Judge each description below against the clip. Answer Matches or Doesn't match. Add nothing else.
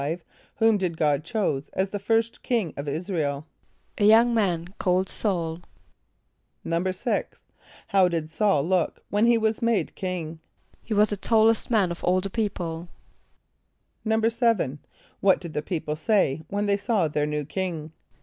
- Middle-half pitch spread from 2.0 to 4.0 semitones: Doesn't match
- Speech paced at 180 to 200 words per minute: Doesn't match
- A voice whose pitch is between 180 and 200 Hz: Matches